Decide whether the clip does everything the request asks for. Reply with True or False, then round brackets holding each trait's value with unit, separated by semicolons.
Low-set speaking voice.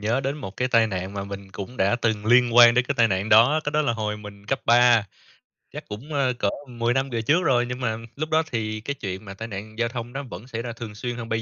True (115 Hz)